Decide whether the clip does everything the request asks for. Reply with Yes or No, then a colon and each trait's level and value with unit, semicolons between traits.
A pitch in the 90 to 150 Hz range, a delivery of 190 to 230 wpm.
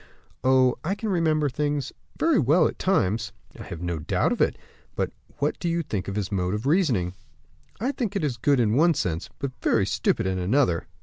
Yes: low, 135 Hz; average, 200 wpm